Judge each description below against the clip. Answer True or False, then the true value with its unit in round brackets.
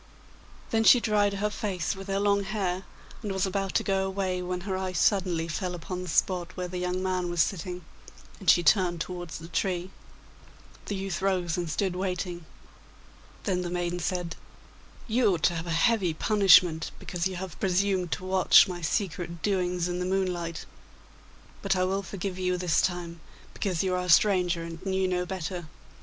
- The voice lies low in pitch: False (180 Hz)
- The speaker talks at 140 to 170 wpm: False (185 wpm)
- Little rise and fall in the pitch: True (1.7 semitones)